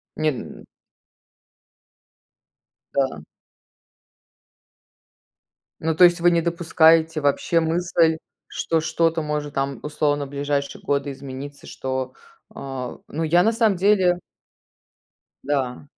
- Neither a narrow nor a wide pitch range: Yes, average, 3.1 semitones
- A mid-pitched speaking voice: Yes, medium, 155 Hz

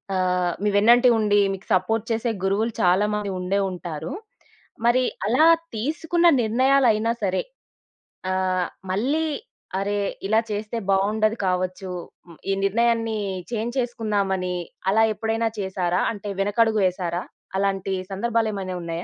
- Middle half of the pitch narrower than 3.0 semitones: No, average, 3.4 semitones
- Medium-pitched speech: No, high, 205 Hz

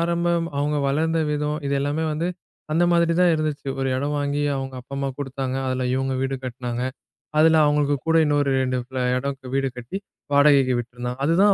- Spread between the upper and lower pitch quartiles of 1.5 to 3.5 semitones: Yes, average, 3.1 semitones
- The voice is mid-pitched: Yes, medium, 145 Hz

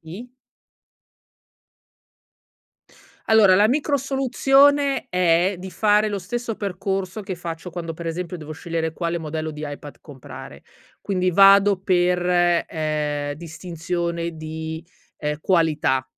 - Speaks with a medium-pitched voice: Yes, medium, 175 Hz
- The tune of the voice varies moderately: Yes, average, 3.7 semitones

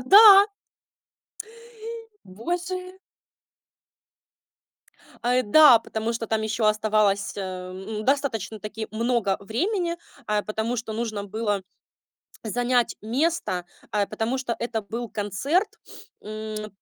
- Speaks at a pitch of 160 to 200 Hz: No, high, 225 Hz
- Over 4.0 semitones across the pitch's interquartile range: No, average, 3.3 semitones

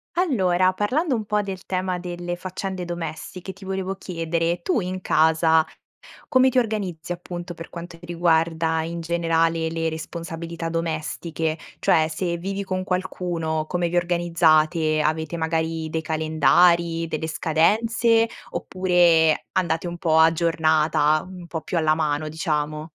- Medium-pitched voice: Yes, medium, 170 Hz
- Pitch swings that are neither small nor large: No, narrow, 2.3 semitones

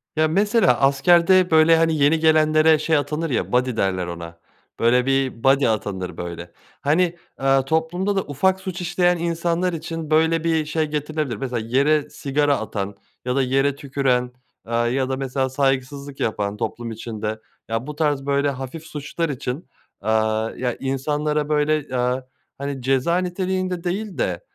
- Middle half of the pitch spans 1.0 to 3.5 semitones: No, average, 4.2 semitones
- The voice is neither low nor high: Yes, medium, 145 Hz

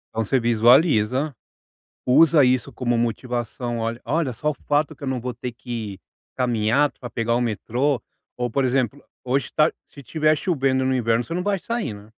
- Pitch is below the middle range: Yes, low, 125 Hz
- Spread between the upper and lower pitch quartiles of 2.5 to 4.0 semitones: Yes, average, 3.6 semitones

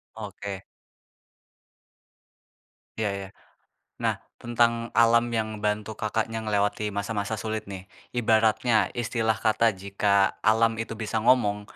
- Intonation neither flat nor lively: No, narrow, 1.7 semitones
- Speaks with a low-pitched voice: Yes, low, 110 Hz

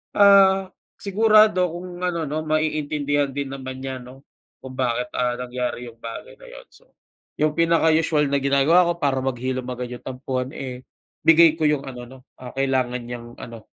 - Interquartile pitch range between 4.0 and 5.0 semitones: Yes, average, 4.3 semitones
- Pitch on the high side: No, low, 135 Hz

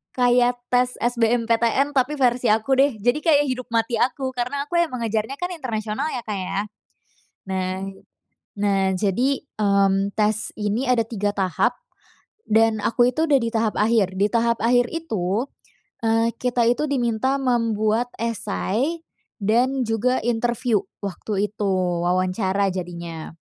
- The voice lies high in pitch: Yes, high, 230 Hz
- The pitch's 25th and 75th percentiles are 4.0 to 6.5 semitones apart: No, average, 3.4 semitones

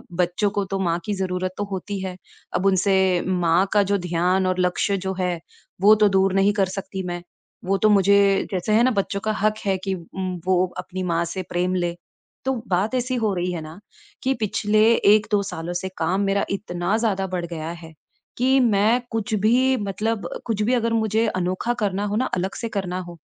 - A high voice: Yes, high, 195 Hz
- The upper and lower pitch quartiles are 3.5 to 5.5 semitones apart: No, average, 2.8 semitones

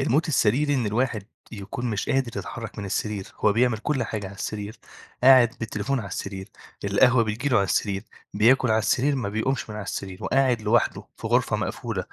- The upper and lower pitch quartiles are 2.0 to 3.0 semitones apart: No, average, 3.7 semitones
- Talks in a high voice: No, low, 110 Hz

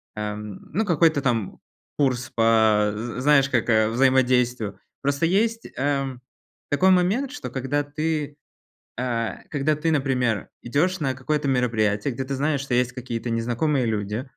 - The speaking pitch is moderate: No, low, 130 Hz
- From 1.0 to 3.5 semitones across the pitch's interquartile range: No, average, 4.2 semitones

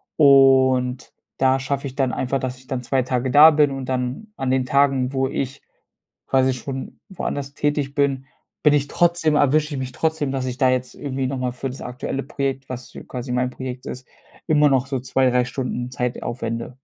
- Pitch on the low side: Yes, low, 130 Hz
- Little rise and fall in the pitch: Yes, narrow, 1.6 semitones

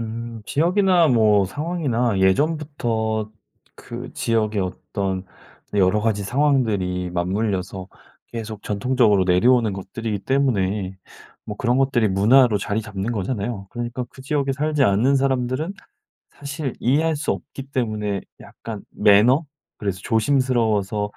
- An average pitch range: Yes, average, 4.8 semitones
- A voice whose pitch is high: No, low, 115 Hz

